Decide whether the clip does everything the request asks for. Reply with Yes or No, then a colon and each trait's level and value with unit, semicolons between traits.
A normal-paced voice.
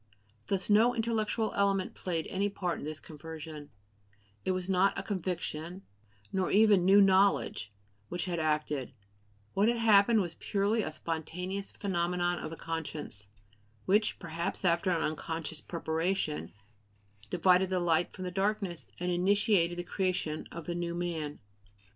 Yes: average, 145 wpm